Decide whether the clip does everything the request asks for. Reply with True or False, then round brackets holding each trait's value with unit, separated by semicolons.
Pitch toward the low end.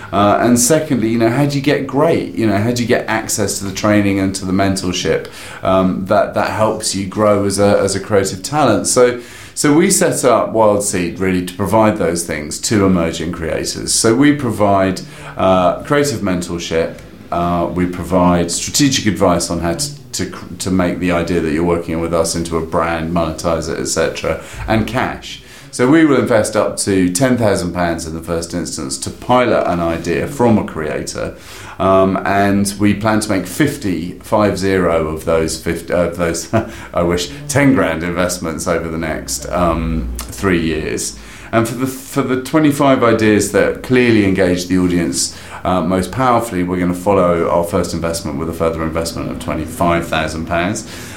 True (95 Hz)